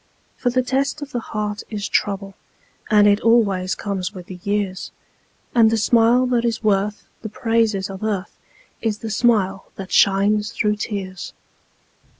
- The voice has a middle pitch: No, high, 210 Hz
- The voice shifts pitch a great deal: No, average, 2.7 semitones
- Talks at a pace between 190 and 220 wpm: No, average, 155 wpm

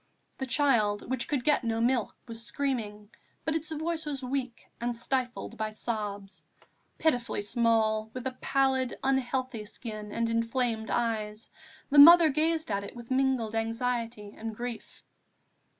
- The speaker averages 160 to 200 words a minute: No, average, 150 wpm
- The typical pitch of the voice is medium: No, high, 240 Hz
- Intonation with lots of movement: No, average, 3.2 semitones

